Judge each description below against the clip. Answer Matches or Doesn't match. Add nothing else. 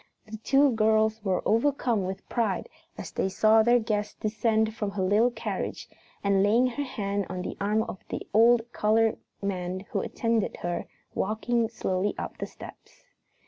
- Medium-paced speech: Matches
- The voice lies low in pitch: Doesn't match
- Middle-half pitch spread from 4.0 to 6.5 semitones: Doesn't match